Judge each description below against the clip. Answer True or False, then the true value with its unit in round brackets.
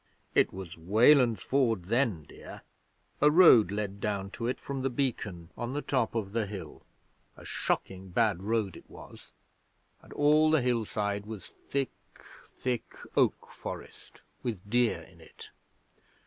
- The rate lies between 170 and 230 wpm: False (150 wpm)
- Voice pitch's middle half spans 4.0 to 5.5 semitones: True (4.3 semitones)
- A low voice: True (110 Hz)